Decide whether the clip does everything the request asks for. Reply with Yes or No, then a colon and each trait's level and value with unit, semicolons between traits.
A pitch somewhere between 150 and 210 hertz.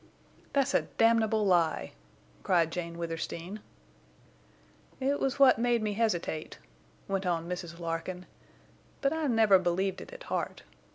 Yes: high, 190 Hz